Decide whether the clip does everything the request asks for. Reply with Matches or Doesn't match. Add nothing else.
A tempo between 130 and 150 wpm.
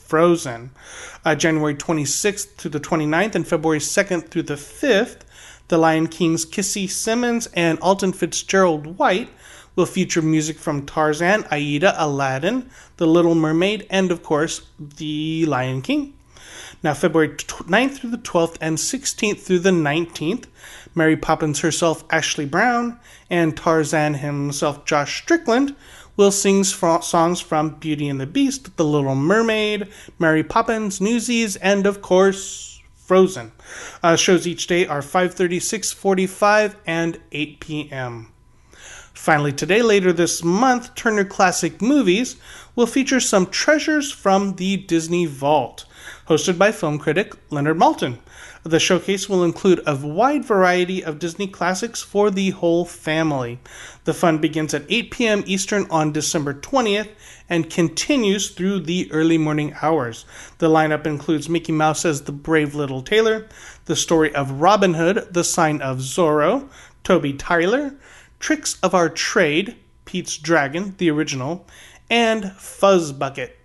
Matches